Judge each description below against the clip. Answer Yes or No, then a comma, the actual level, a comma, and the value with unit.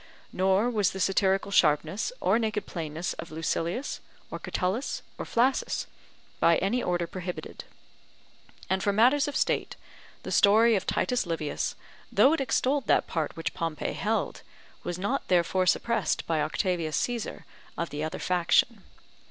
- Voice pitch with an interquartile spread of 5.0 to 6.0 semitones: Yes, average, 5.3 semitones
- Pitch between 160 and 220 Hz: Yes, high, 190 Hz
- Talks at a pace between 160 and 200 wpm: No, average, 145 wpm